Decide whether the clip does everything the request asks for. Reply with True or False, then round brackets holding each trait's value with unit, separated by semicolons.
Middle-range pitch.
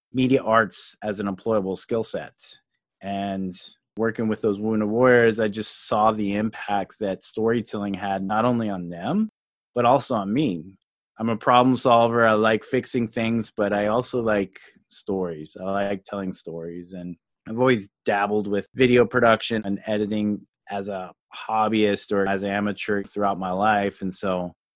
False (105 Hz)